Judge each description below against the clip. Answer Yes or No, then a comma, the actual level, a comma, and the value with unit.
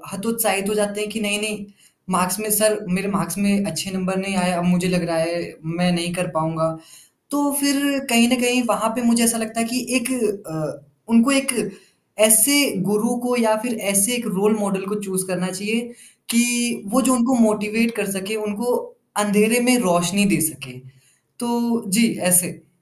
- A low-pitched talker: No, high, 210 Hz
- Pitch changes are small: No, average, 4.0 semitones